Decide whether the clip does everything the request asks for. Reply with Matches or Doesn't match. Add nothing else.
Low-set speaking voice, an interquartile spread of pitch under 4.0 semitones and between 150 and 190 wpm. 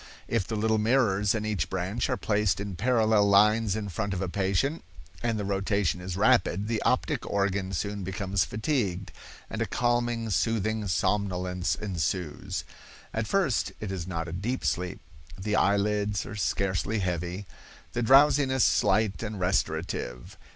Matches